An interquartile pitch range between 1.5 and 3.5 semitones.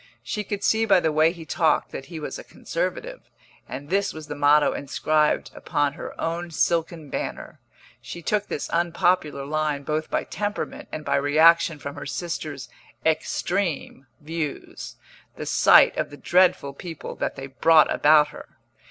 Yes: average, 2.9 semitones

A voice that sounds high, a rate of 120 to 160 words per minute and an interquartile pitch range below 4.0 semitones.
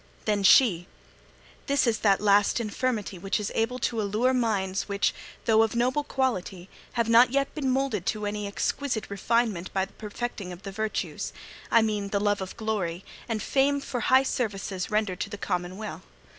No: high, 215 Hz; average, 175 wpm; average, 3.5 semitones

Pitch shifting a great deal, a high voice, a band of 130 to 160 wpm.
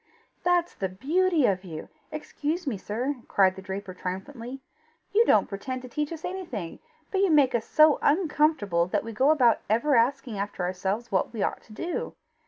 No: wide, 7.5 semitones; high, 245 Hz; average, 185 wpm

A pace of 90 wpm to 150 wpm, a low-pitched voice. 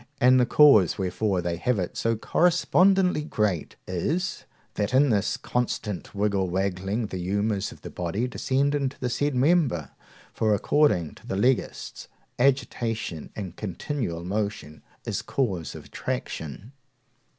Yes: average, 140 wpm; low, 110 Hz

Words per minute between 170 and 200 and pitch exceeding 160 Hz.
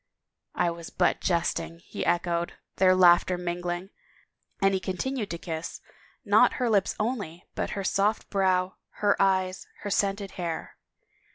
No: average, 155 wpm; medium, 185 Hz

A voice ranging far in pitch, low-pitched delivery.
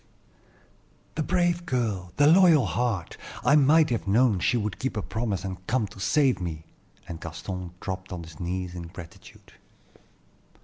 Yes: wide, 6.7 semitones; low, 100 Hz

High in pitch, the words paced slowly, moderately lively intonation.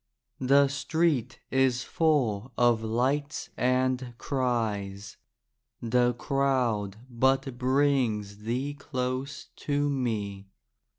No: low, 125 Hz; slow, 85 wpm; average, 3.1 semitones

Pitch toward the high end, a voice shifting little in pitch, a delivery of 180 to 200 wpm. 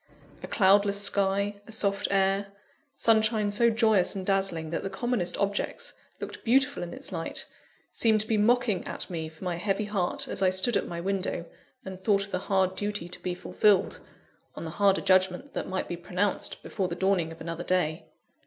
Yes: high, 195 Hz; narrow, 2.3 semitones; average, 190 wpm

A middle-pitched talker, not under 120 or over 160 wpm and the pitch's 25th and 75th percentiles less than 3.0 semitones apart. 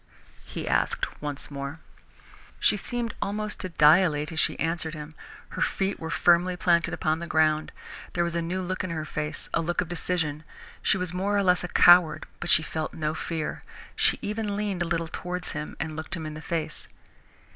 No: medium, 170 Hz; average, 200 wpm; narrow, 2.6 semitones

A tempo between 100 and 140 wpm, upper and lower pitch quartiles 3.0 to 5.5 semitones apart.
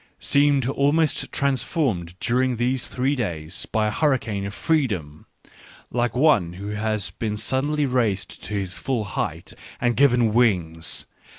Yes: slow, 135 wpm; average, 5.0 semitones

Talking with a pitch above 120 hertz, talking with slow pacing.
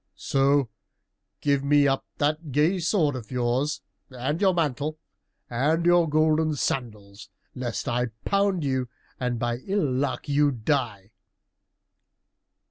Yes: medium, 140 Hz; slow, 125 wpm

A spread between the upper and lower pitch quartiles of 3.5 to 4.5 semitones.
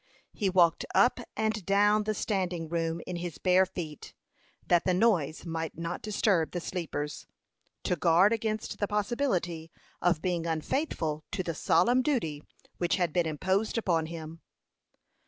Yes: average, 4.1 semitones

